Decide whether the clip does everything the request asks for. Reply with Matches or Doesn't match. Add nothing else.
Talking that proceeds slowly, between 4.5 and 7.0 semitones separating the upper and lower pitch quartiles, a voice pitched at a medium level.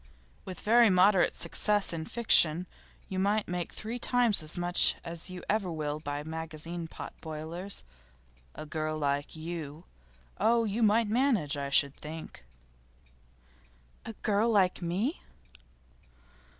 Matches